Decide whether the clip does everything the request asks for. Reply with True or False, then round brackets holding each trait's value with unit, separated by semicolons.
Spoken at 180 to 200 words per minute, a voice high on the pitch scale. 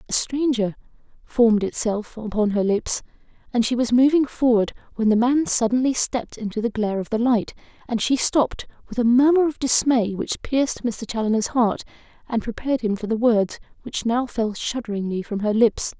True (185 wpm; 230 Hz)